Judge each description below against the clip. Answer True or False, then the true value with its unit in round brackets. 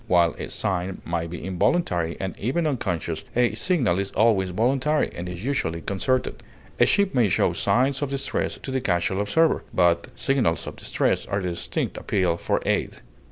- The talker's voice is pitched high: False (100 Hz)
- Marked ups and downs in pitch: True (7.1 semitones)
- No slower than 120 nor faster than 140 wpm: False (175 wpm)